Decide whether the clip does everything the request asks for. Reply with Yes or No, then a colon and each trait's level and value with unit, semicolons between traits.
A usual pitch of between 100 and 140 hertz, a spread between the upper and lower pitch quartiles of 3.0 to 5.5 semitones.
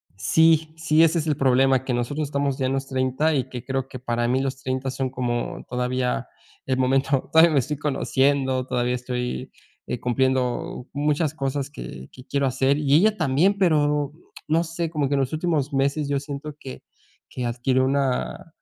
No: low, 135 Hz; narrow, 2.6 semitones